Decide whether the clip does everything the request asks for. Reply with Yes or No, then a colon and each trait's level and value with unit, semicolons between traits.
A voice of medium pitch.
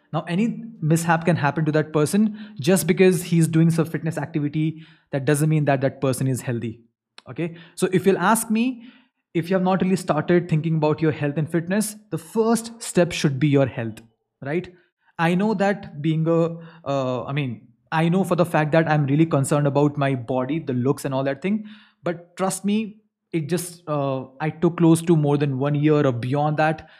Yes: medium, 160 Hz